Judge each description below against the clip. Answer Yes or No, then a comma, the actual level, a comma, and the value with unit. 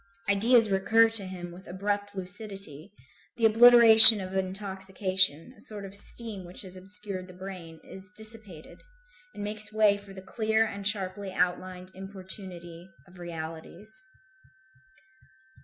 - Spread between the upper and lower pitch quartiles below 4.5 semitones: Yes, narrow, 2.4 semitones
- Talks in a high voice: Yes, high, 195 Hz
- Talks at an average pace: No, slow, 130 wpm